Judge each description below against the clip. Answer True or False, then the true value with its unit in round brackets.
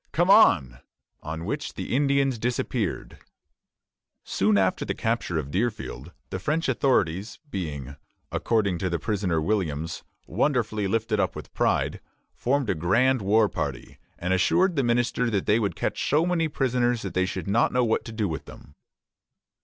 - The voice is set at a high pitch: False (110 Hz)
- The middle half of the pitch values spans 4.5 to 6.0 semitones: True (5.5 semitones)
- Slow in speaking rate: False (160 wpm)